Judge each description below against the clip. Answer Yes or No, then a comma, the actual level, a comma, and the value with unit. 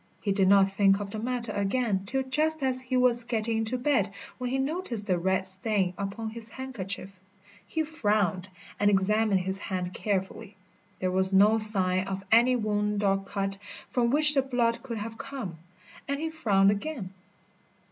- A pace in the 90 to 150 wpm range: No, average, 175 wpm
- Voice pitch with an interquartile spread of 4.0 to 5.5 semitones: Yes, average, 4.3 semitones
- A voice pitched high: Yes, high, 215 Hz